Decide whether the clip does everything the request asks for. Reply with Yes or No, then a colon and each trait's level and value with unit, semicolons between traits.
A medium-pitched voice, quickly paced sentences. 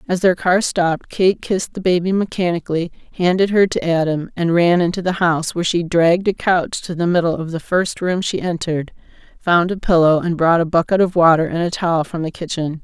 Yes: medium, 175 Hz; fast, 220 wpm